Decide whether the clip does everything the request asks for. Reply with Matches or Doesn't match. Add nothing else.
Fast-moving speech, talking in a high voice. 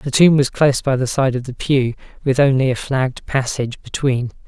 Doesn't match